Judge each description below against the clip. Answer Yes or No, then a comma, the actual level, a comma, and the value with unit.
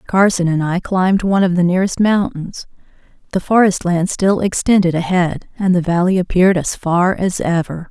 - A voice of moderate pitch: Yes, medium, 180 Hz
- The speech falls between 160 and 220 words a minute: Yes, average, 175 wpm